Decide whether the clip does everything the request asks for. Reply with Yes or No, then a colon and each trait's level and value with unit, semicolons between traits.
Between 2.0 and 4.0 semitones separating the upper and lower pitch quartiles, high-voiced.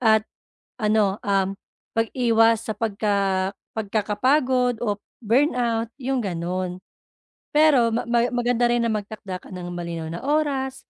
Yes: average, 3.7 semitones; high, 225 Hz